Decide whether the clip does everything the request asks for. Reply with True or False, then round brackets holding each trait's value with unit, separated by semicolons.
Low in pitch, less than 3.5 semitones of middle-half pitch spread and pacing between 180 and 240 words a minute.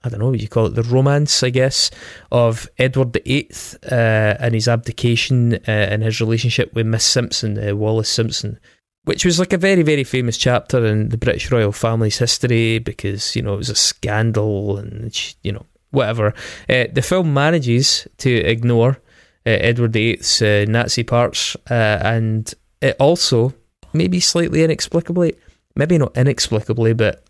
False (115 Hz; 2.8 semitones; 165 wpm)